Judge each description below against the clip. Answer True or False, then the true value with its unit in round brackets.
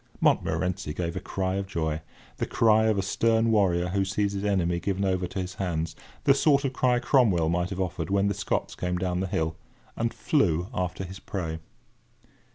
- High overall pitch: False (95 Hz)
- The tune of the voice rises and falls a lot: False (2.8 semitones)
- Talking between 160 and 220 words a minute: True (180 wpm)